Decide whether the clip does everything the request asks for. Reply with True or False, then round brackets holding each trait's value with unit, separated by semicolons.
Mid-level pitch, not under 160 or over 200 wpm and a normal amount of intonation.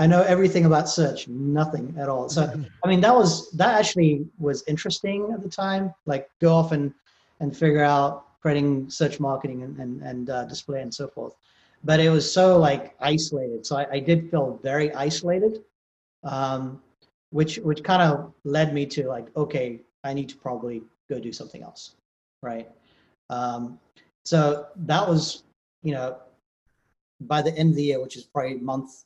True (145 Hz; 180 wpm; 3.2 semitones)